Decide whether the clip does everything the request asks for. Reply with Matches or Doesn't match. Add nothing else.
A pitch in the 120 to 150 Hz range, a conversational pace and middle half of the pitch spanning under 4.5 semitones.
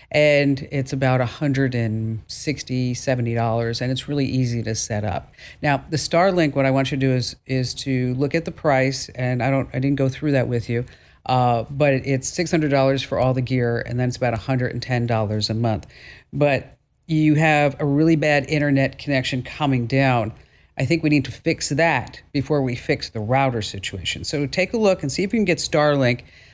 Matches